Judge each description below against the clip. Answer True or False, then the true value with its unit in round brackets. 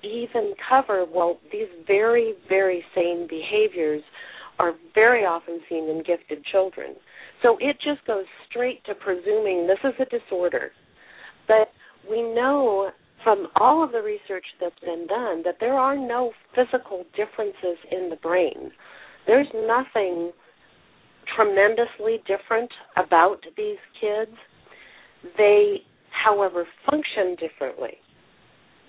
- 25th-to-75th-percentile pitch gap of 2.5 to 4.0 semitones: False (5.3 semitones)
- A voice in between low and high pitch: False (210 Hz)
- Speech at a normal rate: False (120 wpm)